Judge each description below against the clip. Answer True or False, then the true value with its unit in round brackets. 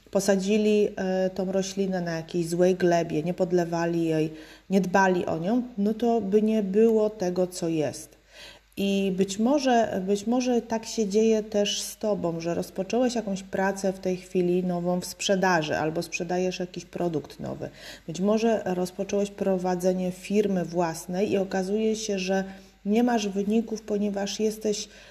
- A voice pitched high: True (195 Hz)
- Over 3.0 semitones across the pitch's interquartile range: False (2.7 semitones)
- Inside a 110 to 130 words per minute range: False (150 wpm)